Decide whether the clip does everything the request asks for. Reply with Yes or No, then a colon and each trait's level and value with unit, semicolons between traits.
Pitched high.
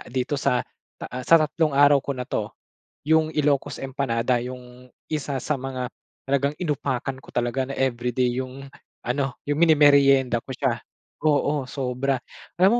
No: low, 135 Hz